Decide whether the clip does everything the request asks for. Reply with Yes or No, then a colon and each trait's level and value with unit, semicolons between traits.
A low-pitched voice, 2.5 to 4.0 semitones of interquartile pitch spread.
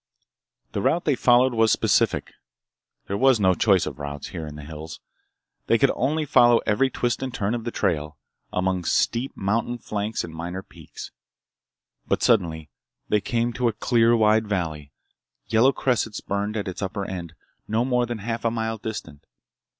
No: low, 105 Hz; average, 4.8 semitones